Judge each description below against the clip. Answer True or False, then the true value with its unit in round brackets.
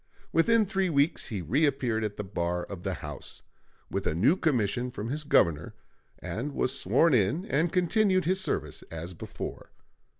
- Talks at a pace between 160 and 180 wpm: True (165 wpm)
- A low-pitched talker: True (130 Hz)